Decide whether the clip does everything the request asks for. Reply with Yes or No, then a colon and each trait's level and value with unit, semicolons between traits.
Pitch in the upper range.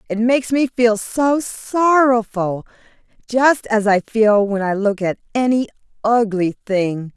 Yes: high, 225 Hz